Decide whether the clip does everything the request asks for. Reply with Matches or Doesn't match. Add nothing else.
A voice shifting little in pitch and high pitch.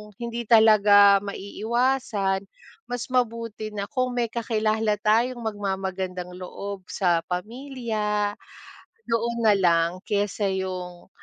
Doesn't match